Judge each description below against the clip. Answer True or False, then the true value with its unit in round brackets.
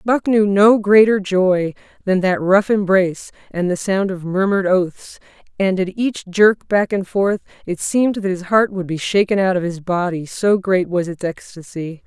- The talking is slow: False (195 wpm)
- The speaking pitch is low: False (190 Hz)